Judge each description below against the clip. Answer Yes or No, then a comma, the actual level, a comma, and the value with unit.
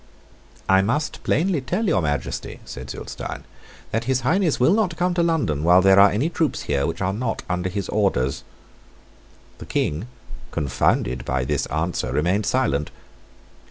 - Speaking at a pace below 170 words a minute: Yes, average, 160 wpm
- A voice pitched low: Yes, low, 100 Hz